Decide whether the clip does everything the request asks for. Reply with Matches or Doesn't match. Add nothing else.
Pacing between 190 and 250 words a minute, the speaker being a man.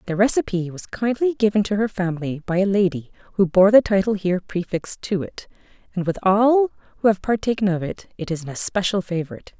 Doesn't match